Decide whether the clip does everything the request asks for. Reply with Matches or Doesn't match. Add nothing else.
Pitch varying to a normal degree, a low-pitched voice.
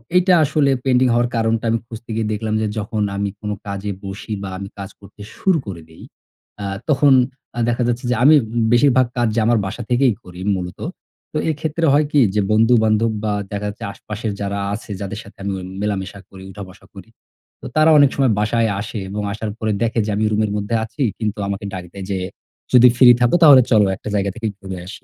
Matches